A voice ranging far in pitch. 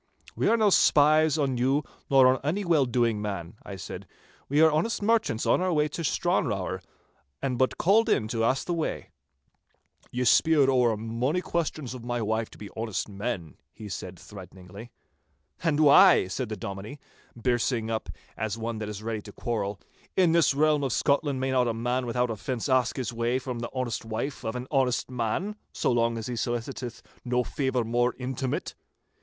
No: average, 4.1 semitones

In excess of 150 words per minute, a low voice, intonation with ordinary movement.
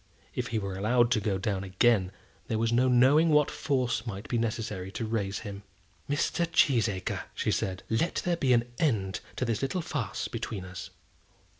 Yes: average, 180 wpm; low, 115 Hz; average, 4.6 semitones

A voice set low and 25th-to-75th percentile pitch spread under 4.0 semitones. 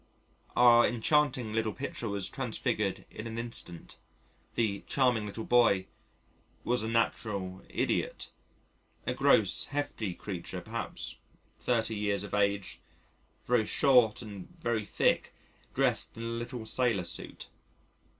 Yes: low, 115 Hz; average, 3.0 semitones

